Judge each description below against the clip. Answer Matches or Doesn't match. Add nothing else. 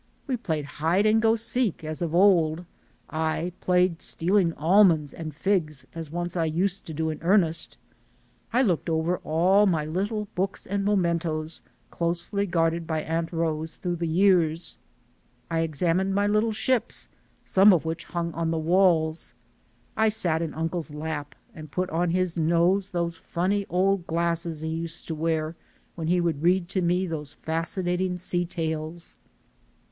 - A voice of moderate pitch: Matches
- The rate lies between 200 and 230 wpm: Doesn't match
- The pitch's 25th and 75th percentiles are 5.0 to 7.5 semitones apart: Doesn't match